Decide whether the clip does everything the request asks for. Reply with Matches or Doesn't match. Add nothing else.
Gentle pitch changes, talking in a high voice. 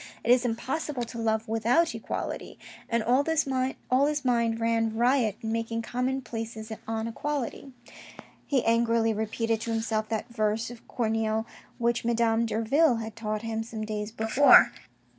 Matches